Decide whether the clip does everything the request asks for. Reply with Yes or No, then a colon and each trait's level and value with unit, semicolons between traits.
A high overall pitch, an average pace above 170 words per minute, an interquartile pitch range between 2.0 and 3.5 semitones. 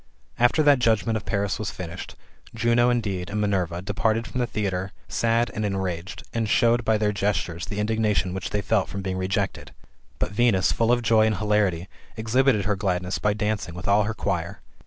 No: low, 105 Hz; average, 195 wpm; average, 3.0 semitones